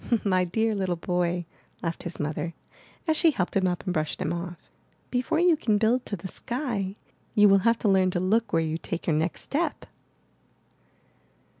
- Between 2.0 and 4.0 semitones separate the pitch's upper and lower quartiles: No, average, 4.7 semitones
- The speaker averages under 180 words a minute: No, average, 185 wpm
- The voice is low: No, high, 190 Hz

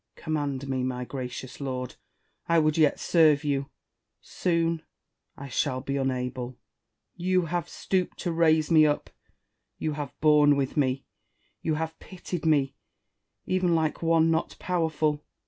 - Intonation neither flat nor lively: Yes, average, 3.2 semitones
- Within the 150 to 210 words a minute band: No, average, 140 wpm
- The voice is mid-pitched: Yes, medium, 150 Hz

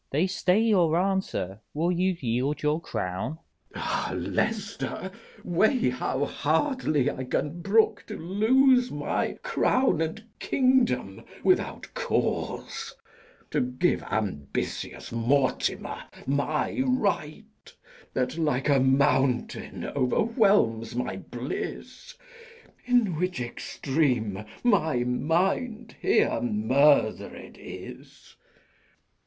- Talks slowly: Yes, slow, 100 wpm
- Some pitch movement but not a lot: No, wide, 8.6 semitones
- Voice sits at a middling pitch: Yes, medium, 160 Hz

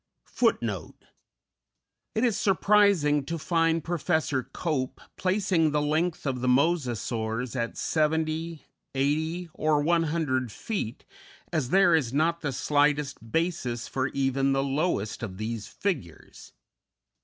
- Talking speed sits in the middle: No, slow, 115 wpm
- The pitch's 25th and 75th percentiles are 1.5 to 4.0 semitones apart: No, average, 4.4 semitones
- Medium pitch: Yes, medium, 150 Hz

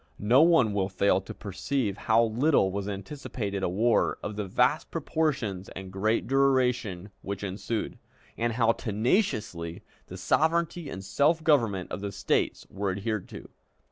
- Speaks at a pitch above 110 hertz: No, low, 105 Hz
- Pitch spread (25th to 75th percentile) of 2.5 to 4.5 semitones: No, average, 5.1 semitones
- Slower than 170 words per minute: Yes, average, 150 wpm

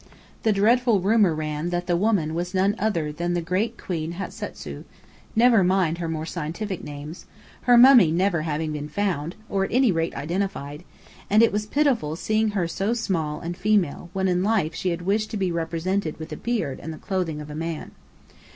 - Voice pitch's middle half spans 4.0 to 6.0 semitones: Yes, average, 4.4 semitones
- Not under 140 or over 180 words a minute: No, average, 195 wpm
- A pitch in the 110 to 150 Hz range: No, medium, 180 Hz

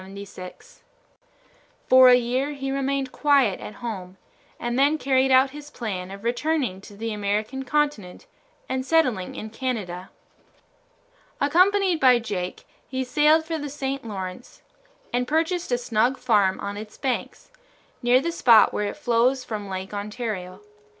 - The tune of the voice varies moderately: Yes, average, 4.8 semitones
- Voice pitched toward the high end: Yes, very high, 250 Hz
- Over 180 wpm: No, average, 145 wpm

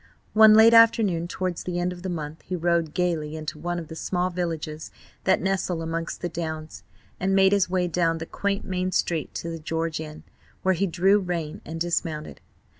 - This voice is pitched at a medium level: Yes, medium, 175 Hz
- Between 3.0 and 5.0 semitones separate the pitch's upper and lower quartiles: No, narrow, 2.4 semitones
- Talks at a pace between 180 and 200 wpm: Yes, average, 195 wpm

